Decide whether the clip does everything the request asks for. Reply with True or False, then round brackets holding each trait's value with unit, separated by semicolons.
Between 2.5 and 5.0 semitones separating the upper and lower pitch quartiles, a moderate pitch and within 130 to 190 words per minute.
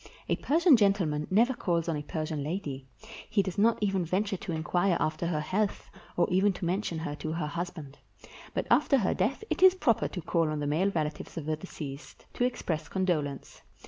False (4.5 semitones; 175 Hz; 200 wpm)